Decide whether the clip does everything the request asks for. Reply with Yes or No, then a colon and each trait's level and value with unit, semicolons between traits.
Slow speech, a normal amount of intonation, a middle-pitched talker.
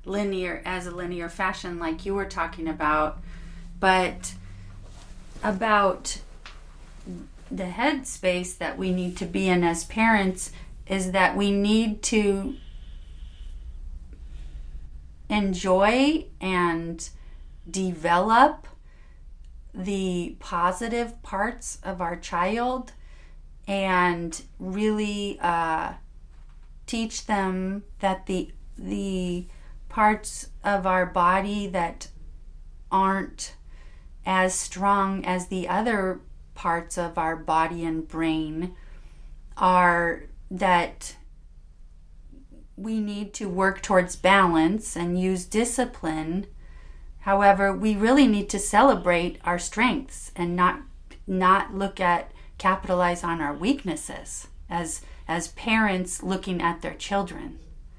Yes: slow, 100 wpm; average, 4.4 semitones; medium, 180 Hz